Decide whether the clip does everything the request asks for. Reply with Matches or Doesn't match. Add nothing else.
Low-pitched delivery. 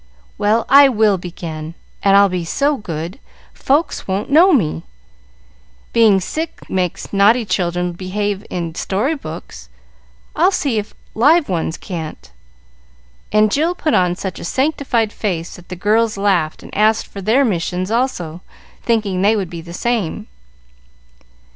Doesn't match